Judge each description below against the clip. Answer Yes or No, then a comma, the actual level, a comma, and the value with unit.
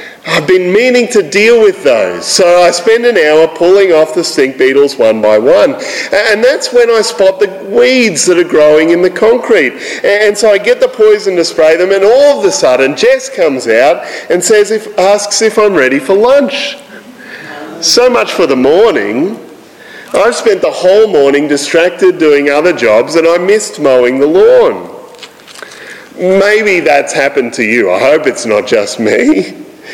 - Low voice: No, high, 210 Hz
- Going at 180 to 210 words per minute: Yes, average, 190 wpm